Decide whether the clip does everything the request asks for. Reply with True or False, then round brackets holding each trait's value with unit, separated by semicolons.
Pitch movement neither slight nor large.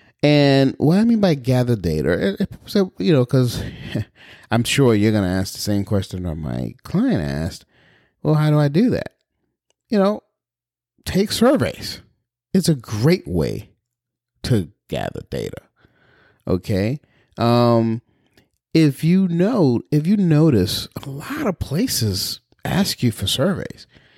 False (6.9 semitones)